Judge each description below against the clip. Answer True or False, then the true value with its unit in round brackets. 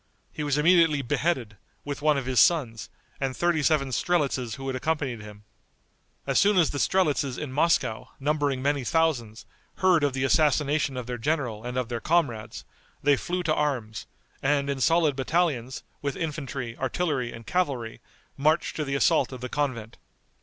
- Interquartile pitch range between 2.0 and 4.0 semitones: True (3.6 semitones)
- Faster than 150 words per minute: True (170 wpm)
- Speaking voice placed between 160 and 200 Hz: False (140 Hz)